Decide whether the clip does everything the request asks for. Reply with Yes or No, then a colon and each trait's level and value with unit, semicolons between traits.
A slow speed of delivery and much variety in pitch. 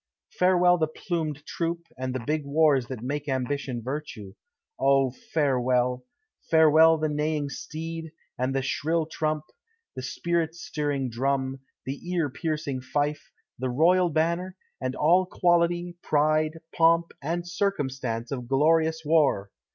No: slow, 130 wpm; average, 3.7 semitones